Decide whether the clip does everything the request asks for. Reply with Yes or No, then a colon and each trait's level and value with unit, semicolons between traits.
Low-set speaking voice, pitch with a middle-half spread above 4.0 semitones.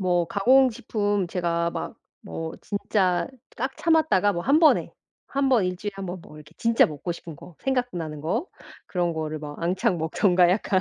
No: medium, 185 Hz; wide, 5.4 semitones